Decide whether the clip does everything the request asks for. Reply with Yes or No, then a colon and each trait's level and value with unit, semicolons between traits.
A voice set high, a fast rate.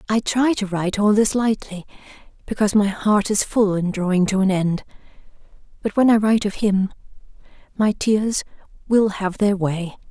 No: high, 205 Hz; average, 170 wpm